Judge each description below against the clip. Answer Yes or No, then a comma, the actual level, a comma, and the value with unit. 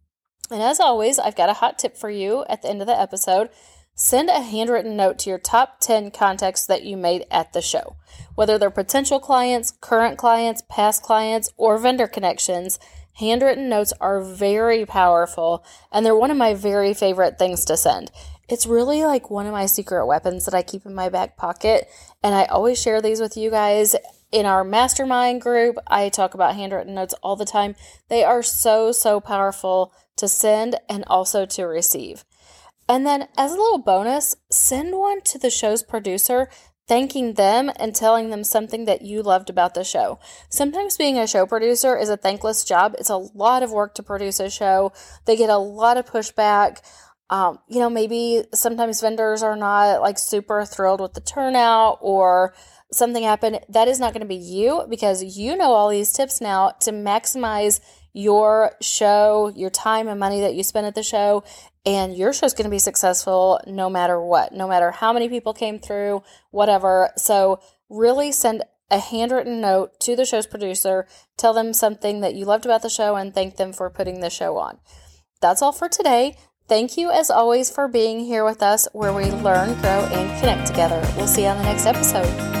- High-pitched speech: Yes, high, 210 Hz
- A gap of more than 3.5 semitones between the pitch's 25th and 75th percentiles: No, average, 3.2 semitones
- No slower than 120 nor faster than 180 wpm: No, average, 195 wpm